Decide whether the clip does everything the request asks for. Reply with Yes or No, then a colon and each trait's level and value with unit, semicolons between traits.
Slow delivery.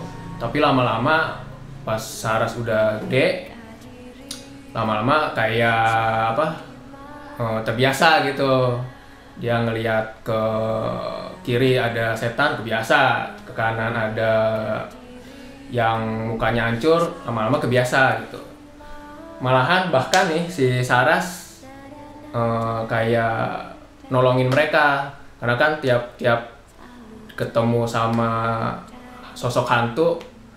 Yes: slow, 80 wpm